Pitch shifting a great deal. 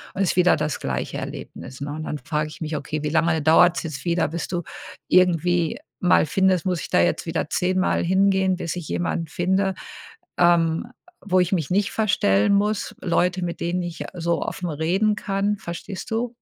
No: average, 2.8 semitones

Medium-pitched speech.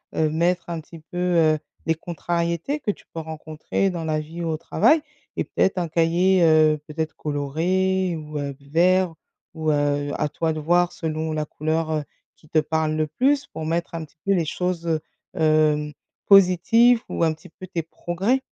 Yes: medium, 165 Hz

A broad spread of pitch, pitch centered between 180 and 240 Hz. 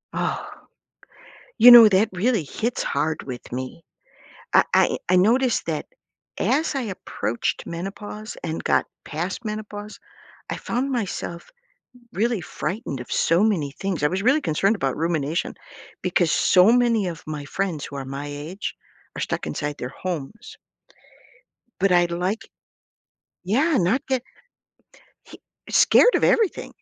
Yes: wide, 6.3 semitones; high, 190 Hz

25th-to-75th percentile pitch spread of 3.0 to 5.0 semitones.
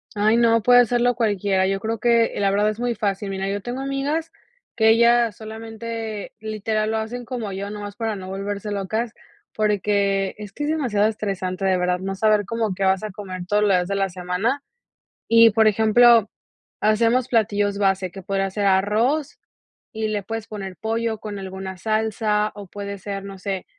No: narrow, 2.5 semitones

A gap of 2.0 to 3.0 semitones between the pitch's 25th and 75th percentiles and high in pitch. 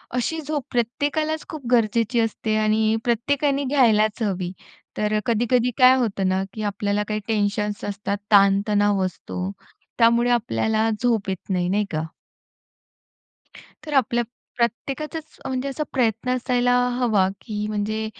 No: average, 3.5 semitones; high, 225 Hz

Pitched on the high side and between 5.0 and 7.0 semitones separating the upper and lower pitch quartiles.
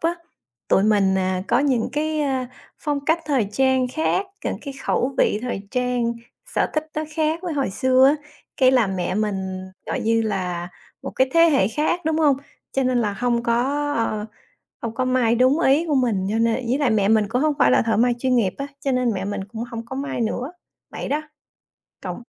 No: very high, 250 Hz; average, 4.5 semitones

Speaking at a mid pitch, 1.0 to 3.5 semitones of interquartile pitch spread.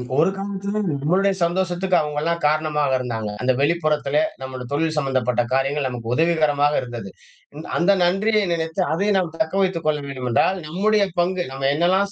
No: medium, 160 Hz; average, 5.1 semitones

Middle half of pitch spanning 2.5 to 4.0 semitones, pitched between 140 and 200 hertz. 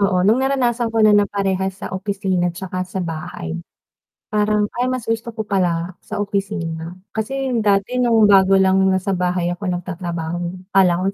Yes: average, 2.9 semitones; high, 190 Hz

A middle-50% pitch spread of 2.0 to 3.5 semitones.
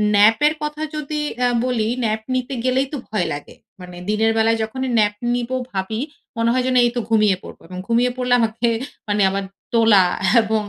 Yes: average, 2.8 semitones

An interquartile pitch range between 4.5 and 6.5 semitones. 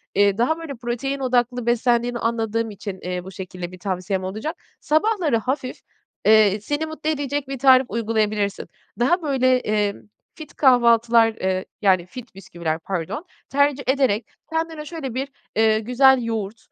Yes: average, 4.9 semitones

